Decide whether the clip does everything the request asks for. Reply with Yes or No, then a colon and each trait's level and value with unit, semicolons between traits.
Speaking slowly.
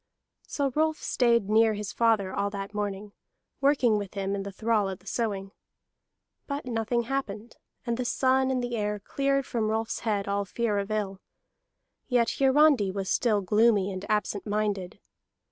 No: average, 165 wpm